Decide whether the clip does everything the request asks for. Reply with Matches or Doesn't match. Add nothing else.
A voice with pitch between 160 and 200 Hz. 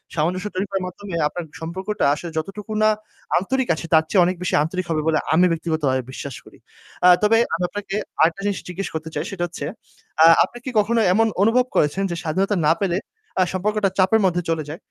Matches